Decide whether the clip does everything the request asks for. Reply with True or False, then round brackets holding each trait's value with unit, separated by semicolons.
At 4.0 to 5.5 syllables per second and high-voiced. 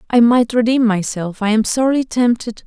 True (5.3 syllables/s; 230 Hz)